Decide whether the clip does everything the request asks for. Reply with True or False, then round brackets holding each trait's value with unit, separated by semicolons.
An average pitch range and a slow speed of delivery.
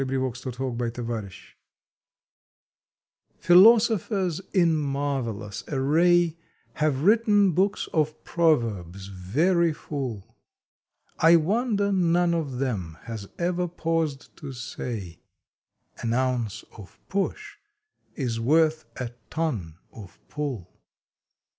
False (6.6 semitones; 95 wpm)